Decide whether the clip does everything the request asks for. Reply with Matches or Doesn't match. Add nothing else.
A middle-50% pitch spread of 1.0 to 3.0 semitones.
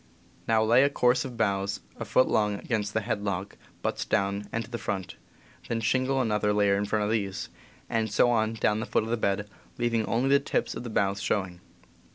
Matches